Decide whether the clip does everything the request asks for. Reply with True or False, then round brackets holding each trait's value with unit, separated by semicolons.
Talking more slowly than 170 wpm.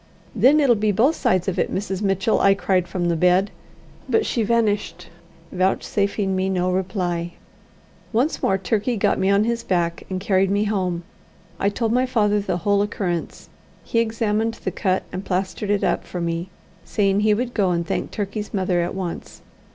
False (180 wpm)